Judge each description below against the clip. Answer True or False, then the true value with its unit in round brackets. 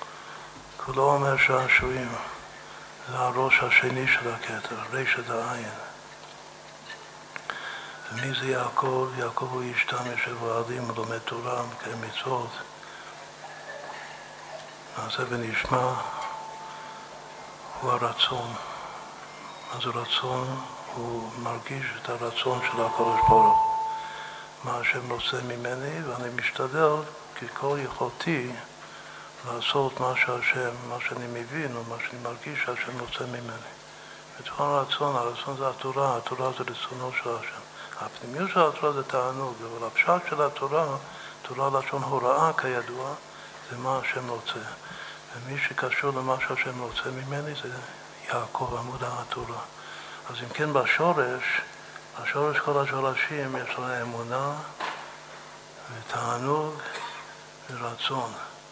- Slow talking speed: False (110 wpm)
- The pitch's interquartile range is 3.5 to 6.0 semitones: False (2.7 semitones)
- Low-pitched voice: True (130 Hz)